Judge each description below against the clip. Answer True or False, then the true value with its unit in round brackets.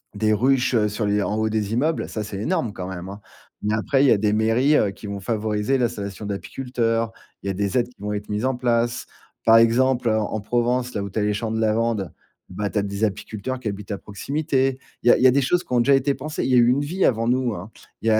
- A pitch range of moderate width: True (3.4 semitones)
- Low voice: True (115 Hz)